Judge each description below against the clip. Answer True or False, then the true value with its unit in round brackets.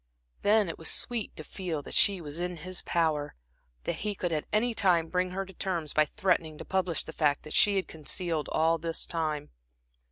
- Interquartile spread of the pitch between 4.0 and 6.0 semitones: False (3.3 semitones)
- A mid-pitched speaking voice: True (170 Hz)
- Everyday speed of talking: False (210 wpm)